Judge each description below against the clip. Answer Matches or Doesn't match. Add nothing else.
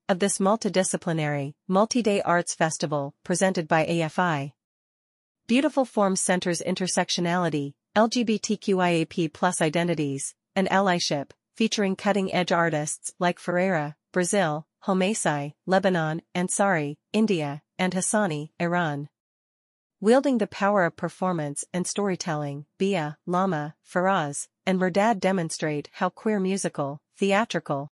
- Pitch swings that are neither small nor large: Matches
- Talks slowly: Matches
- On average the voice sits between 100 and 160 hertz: Doesn't match